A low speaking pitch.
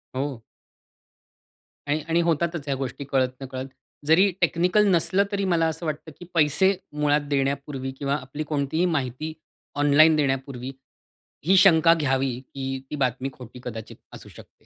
No: medium, 145 Hz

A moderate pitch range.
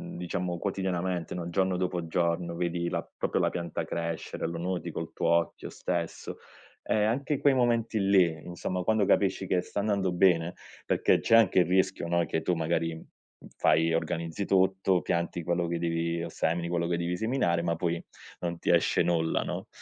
No: narrow, 2.0 semitones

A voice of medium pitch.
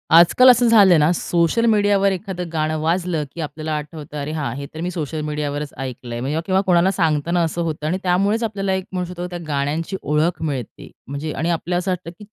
Yes: medium, 170 Hz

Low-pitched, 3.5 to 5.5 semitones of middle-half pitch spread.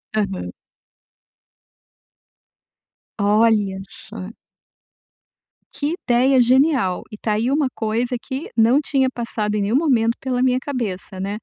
No: high, 235 Hz; average, 3.9 semitones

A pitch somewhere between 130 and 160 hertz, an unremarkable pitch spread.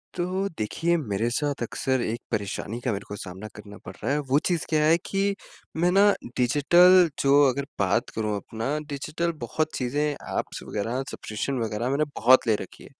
No: low, 135 Hz; wide, 6.1 semitones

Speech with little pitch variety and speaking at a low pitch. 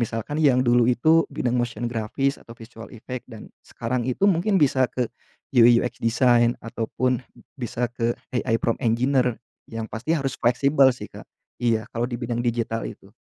Yes: narrow, 1.8 semitones; low, 120 Hz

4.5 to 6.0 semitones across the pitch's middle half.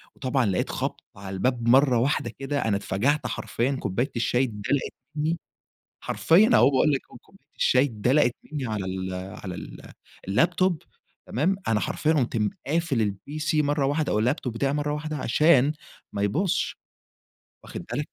Yes: average, 5.2 semitones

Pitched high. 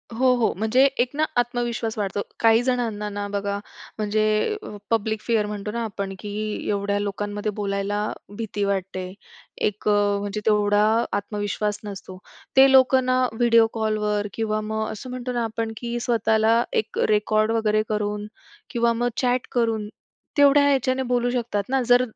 Yes: high, 220 Hz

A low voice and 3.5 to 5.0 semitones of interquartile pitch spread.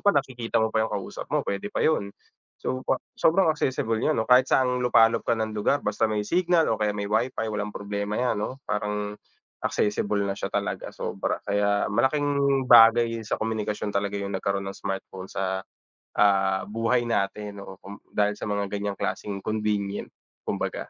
No: low, 105 Hz; average, 2.8 semitones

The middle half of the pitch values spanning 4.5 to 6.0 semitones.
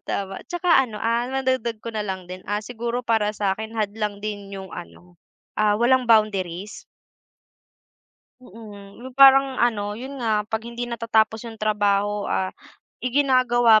No: average, 2.9 semitones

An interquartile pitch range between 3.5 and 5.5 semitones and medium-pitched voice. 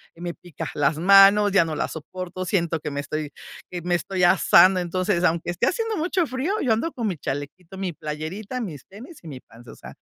Yes: average, 4.2 semitones; medium, 180 Hz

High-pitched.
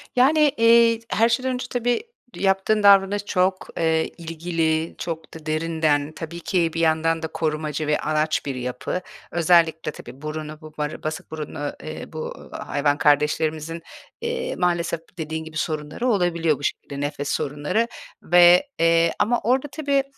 No: medium, 165 Hz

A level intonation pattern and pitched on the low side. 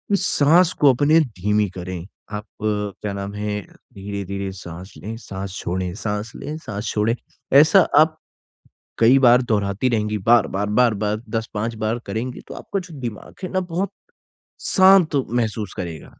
No: average, 4.3 semitones; low, 105 Hz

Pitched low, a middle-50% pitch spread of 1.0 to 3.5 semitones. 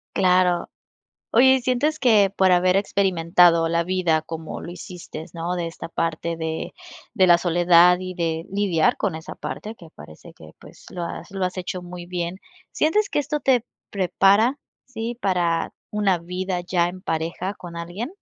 No: medium, 180 Hz; average, 2.8 semitones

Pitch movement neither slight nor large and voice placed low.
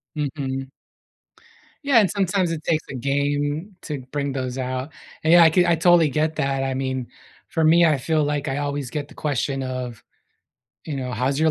No: average, 3.1 semitones; medium, 145 Hz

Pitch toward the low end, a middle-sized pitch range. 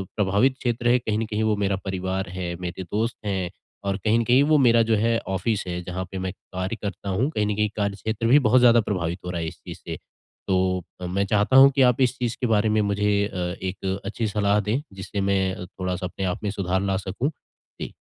Yes: low, 100 Hz; average, 3.4 semitones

